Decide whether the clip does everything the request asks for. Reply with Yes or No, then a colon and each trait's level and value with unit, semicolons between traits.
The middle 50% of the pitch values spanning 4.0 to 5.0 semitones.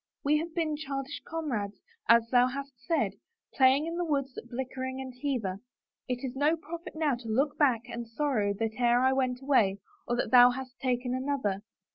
No: average, 3.0 semitones